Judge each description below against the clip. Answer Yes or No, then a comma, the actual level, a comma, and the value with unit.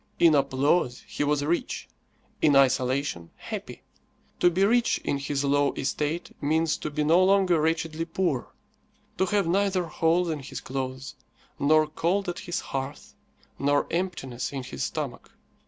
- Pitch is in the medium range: Yes, medium, 155 Hz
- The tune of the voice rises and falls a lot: No, average, 3.9 semitones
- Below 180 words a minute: Yes, average, 150 wpm